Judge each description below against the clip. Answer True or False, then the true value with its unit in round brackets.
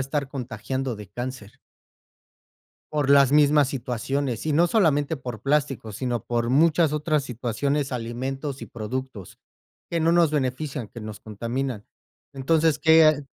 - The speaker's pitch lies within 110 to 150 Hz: True (135 Hz)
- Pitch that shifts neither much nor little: True (3.7 semitones)